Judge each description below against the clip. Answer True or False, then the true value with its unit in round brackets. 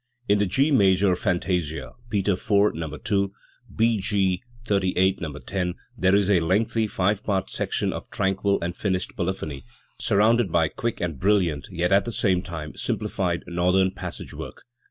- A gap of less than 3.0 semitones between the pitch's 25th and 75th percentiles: True (2.5 semitones)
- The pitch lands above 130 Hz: False (95 Hz)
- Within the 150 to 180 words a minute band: True (160 wpm)